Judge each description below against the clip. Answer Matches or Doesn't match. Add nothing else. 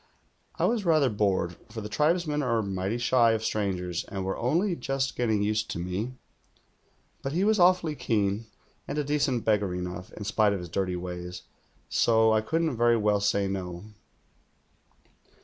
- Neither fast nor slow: Matches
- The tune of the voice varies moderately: Doesn't match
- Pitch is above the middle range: Doesn't match